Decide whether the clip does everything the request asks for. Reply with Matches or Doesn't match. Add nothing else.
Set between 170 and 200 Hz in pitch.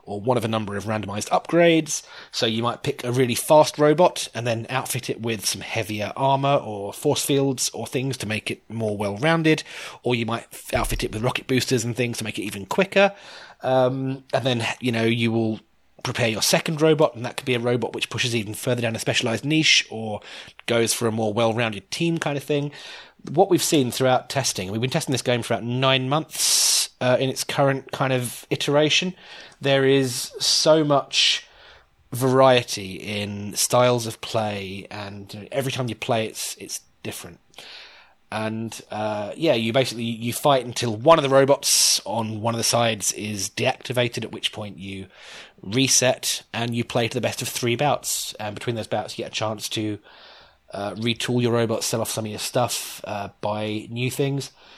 Doesn't match